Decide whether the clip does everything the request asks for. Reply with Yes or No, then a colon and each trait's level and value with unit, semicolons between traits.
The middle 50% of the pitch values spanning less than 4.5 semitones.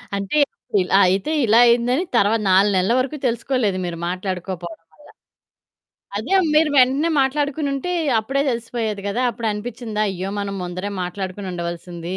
No: average, 5.2 semitones